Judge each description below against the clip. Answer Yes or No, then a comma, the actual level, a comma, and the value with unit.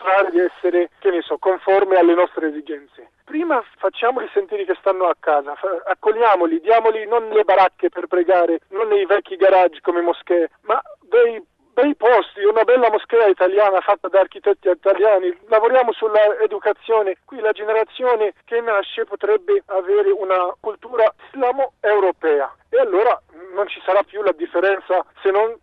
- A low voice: No, high, 205 Hz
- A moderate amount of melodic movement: Yes, average, 4.0 semitones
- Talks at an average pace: Yes, average, 150 wpm